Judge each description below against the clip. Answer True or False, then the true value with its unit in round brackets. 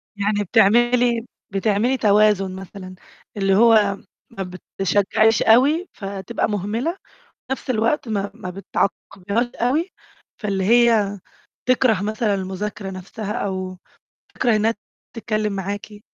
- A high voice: True (210 Hz)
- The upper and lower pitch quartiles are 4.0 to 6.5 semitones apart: False (2.9 semitones)